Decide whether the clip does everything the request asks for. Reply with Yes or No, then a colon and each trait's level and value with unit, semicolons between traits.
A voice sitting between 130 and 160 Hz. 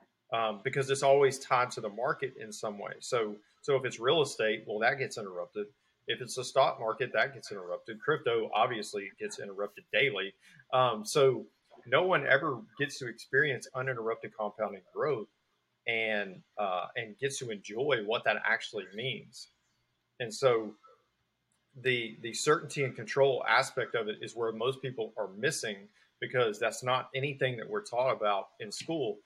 Yes: low, 135 Hz